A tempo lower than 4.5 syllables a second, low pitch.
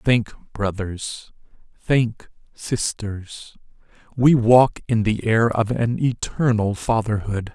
Yes: 3.1 syllables/s; low, 110 Hz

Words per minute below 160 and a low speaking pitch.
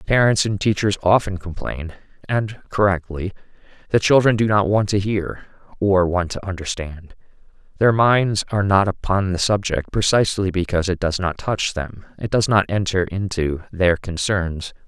Yes: average, 150 wpm; very low, 95 Hz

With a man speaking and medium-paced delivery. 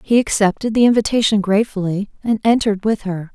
No: female; average, 160 wpm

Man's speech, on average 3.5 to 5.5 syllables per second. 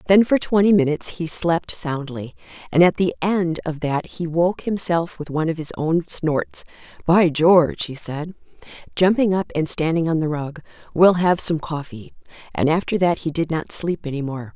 No: female; 4.8 syllables/s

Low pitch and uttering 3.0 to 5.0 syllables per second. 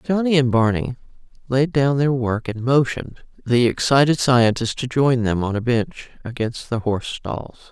Yes: low, 125 Hz; 4.8 syllables/s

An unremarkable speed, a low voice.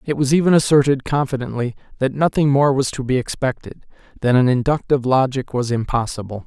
Yes: average, 160 wpm; low, 130 Hz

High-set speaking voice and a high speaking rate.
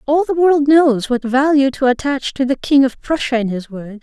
Yes: very high, 270 Hz; fast, 240 wpm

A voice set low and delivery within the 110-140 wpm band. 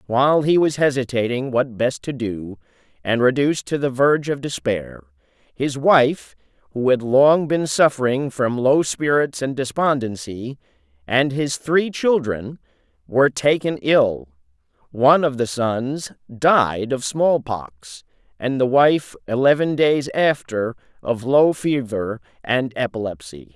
Yes: low, 130 Hz; slow, 135 wpm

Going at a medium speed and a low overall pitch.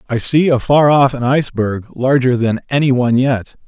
Yes: average, 180 wpm; low, 130 Hz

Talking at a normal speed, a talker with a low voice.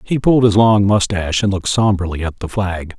No: fast, 220 wpm; low, 100 Hz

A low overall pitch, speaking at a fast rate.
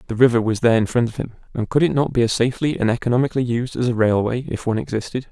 Yes: low, 120 Hz; fast, 270 wpm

